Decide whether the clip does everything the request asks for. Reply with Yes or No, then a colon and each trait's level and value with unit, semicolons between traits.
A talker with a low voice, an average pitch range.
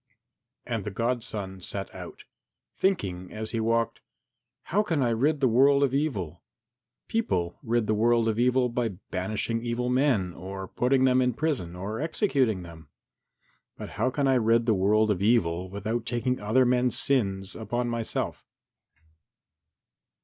Yes: low, 115 Hz; average, 4.2 semitones